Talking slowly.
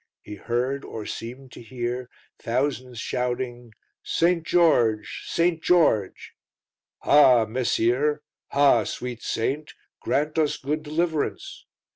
Yes: slow, 105 wpm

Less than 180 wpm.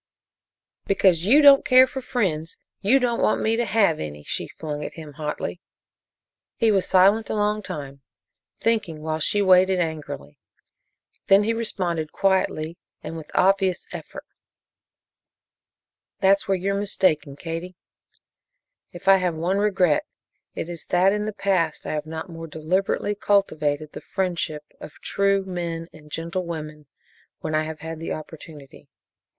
Yes: average, 150 wpm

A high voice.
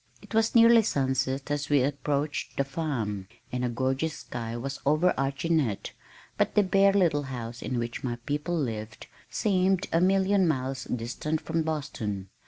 No: medium, 140 Hz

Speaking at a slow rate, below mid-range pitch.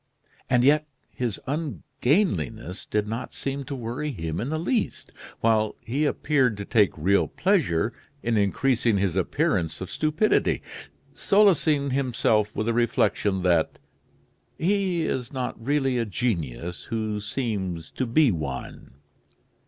Yes: slow, 130 wpm; low, 115 Hz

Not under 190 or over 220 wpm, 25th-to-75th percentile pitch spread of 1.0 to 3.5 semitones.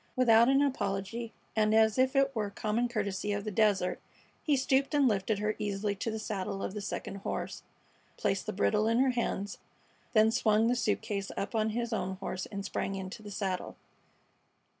Yes: average, 195 wpm; average, 3.0 semitones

